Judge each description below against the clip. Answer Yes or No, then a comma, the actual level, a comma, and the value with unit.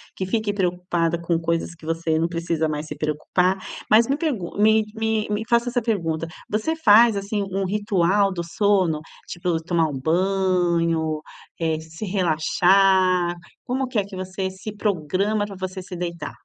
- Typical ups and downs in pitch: Yes, average, 3.7 semitones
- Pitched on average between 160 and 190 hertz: Yes, medium, 185 Hz